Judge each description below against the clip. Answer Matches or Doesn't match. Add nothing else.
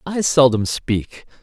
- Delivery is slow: Matches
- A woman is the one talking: Doesn't match